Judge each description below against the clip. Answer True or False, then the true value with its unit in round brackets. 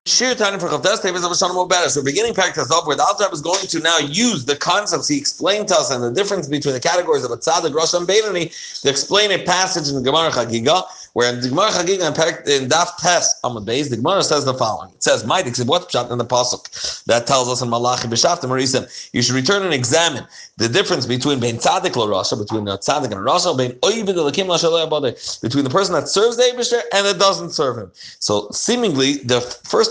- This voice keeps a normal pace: False (210 wpm)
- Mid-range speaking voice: True (165 Hz)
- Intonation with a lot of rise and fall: True (6.7 semitones)